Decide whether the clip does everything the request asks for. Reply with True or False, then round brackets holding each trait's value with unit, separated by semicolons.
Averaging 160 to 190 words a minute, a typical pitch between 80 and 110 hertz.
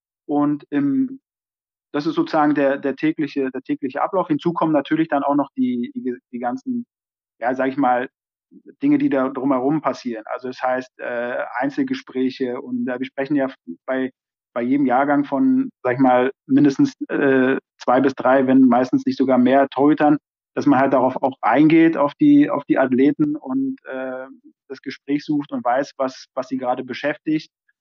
False (180 wpm; 140 Hz)